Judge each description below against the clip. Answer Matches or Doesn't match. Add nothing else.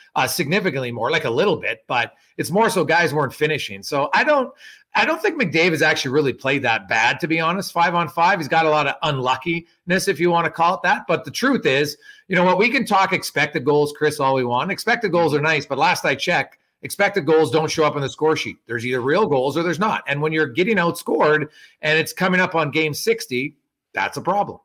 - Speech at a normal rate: Doesn't match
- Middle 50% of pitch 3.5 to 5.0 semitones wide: Matches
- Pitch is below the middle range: Doesn't match